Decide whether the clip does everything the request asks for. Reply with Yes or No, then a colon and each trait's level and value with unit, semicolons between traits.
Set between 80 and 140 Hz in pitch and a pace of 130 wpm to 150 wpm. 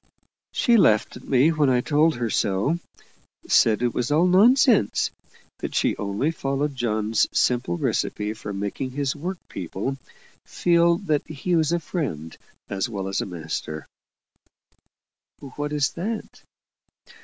Yes: low, 135 Hz; average, 140 wpm